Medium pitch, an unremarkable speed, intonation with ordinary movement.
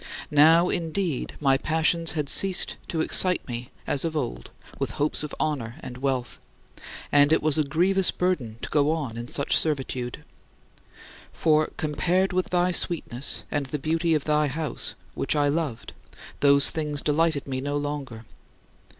Yes: medium, 150 Hz; average, 160 wpm; average, 3.0 semitones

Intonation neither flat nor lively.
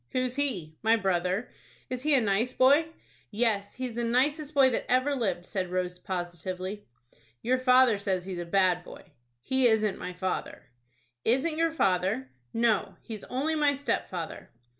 No: wide, 5.8 semitones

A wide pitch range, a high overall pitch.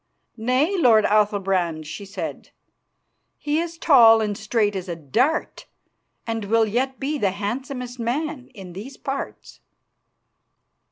No: average, 5.0 semitones; high, 225 Hz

